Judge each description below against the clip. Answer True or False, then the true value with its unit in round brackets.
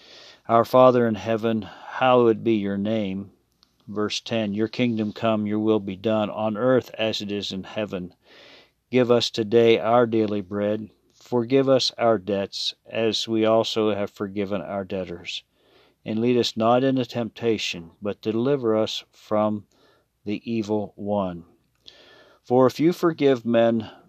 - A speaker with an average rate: True (145 wpm)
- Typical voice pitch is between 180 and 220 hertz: False (110 Hz)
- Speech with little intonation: True (2.3 semitones)